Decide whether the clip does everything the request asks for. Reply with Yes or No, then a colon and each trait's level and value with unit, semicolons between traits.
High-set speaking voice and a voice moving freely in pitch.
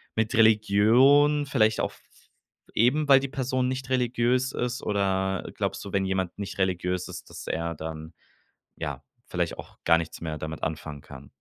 No: low, 105 Hz; wide, 7.2 semitones